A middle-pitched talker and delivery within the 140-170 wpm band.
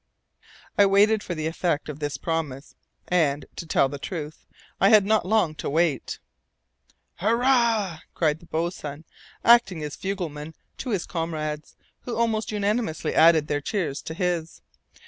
Yes: medium, 170 Hz; average, 145 wpm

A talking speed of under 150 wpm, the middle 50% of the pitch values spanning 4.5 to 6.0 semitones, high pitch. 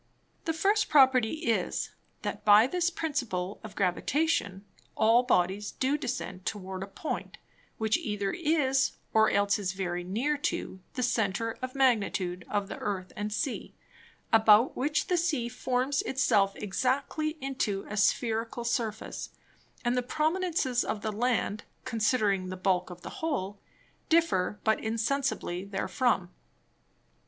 Yes: average, 140 wpm; average, 5.3 semitones; high, 225 Hz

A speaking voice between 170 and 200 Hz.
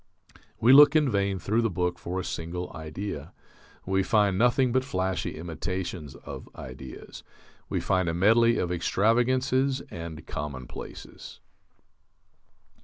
No: very low, 95 Hz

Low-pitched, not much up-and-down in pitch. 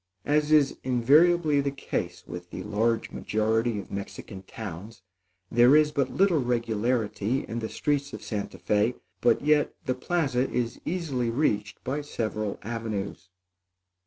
No: low, 120 Hz; average, 4.9 semitones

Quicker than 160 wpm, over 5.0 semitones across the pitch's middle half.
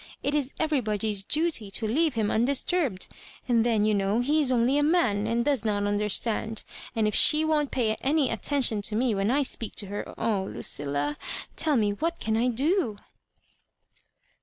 Yes: average, 180 wpm; wide, 5.4 semitones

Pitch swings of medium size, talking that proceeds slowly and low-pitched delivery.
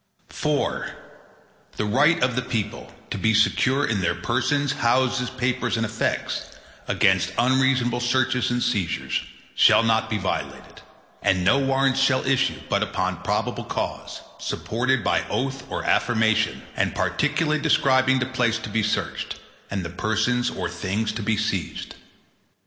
No: average, 3.4 semitones; average, 145 wpm; low, 120 Hz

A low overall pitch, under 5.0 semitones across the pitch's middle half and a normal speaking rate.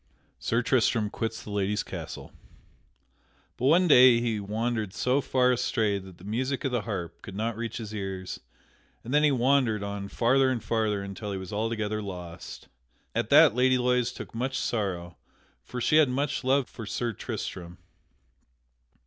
Yes: low, 115 Hz; average, 3.8 semitones; average, 170 wpm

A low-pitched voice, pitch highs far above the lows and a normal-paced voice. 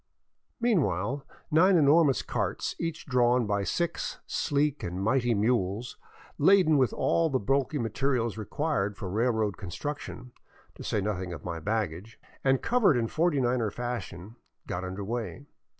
Yes: low, 120 Hz; wide, 6.1 semitones; average, 145 wpm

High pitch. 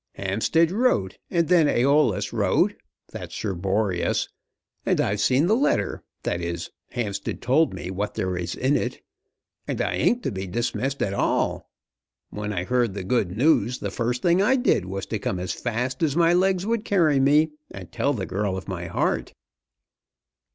No: low, 120 Hz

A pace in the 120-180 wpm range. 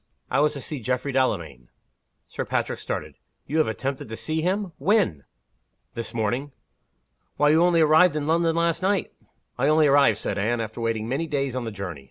No: average, 190 wpm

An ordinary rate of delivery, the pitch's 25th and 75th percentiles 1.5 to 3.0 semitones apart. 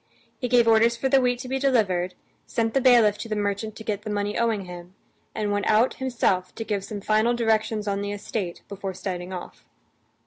No: fast, 210 wpm; average, 2.7 semitones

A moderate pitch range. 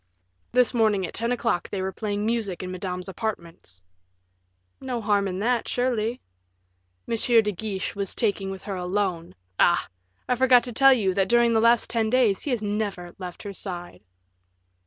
Yes: average, 3.8 semitones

